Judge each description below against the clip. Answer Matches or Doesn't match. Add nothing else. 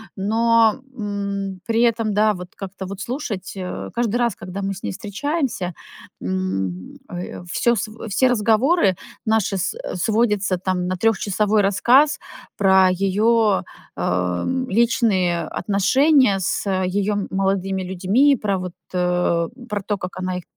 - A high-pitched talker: Matches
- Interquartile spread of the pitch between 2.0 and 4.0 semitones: Matches